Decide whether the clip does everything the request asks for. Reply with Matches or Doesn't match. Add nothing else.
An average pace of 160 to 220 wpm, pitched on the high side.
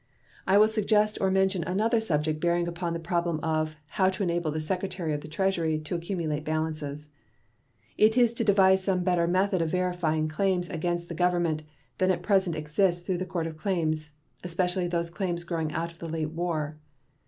Doesn't match